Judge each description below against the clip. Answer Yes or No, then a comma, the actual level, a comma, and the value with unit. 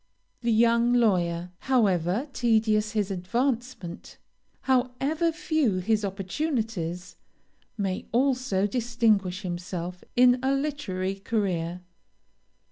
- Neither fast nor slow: No, slow, 90 wpm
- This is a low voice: No, high, 215 Hz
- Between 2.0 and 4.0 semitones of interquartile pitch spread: No, average, 5.1 semitones